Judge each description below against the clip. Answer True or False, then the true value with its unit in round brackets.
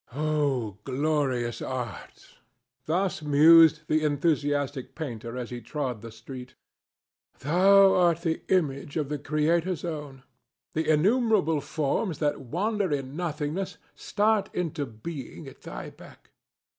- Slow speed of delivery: True (120 wpm)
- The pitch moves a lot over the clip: False (4.0 semitones)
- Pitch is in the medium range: True (150 Hz)